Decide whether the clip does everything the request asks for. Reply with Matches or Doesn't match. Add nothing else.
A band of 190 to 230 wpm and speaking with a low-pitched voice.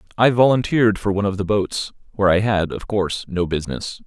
Matches